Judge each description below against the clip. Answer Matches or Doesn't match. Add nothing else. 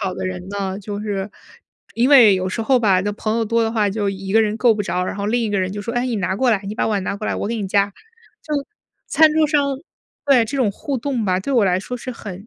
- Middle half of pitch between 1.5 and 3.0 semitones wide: Doesn't match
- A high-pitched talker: Matches